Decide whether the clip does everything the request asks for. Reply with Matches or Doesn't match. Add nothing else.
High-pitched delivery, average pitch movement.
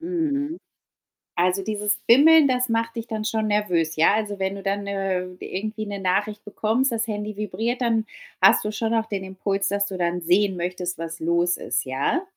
Matches